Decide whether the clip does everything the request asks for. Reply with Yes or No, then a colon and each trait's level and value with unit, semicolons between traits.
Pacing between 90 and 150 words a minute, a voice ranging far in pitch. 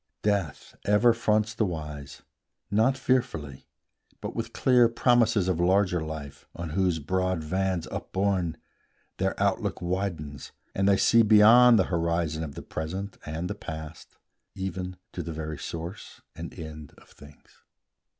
No: average, 145 wpm; average, 4.6 semitones